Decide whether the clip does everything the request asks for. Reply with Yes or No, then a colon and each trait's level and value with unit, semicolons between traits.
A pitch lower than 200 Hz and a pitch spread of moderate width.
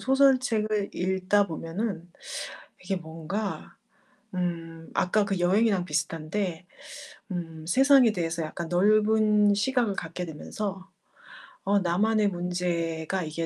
Yes: medium, 185 Hz; average, 4.1 semitones